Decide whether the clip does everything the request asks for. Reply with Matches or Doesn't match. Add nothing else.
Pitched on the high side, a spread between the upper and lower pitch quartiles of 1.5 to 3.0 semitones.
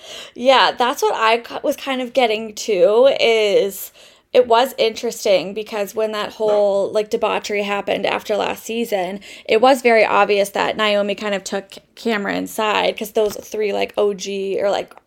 Matches